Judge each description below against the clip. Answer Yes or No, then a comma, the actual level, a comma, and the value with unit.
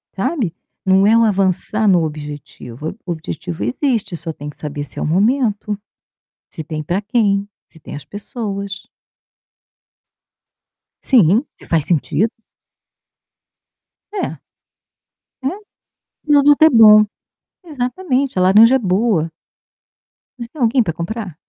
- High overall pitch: Yes, high, 200 Hz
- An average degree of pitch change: No, wide, 6.3 semitones